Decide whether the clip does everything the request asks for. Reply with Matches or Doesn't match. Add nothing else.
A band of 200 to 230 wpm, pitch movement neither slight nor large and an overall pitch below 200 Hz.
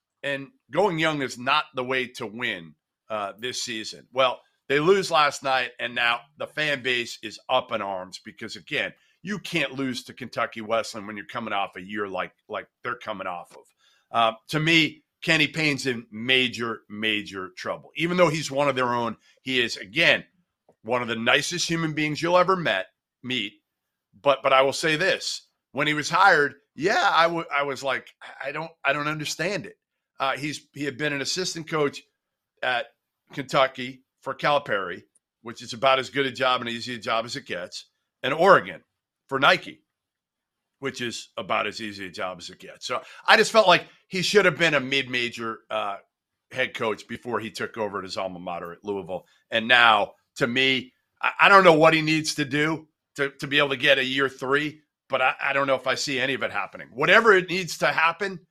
Matches